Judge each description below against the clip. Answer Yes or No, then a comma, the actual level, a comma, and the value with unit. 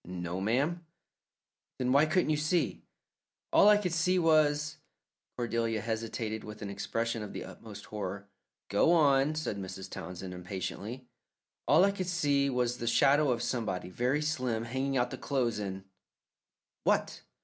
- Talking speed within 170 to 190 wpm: No, average, 160 wpm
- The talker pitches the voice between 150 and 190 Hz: No, low, 125 Hz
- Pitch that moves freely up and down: Yes, wide, 6.1 semitones